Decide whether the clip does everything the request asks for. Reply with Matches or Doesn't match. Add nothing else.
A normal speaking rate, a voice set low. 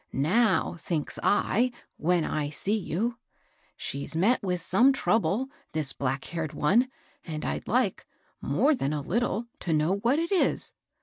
Doesn't match